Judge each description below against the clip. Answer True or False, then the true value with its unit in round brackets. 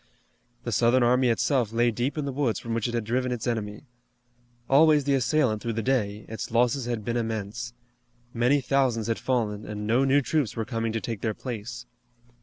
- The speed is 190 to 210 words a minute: True (200 wpm)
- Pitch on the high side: False (120 Hz)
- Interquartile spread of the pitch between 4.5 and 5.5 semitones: False (2.5 semitones)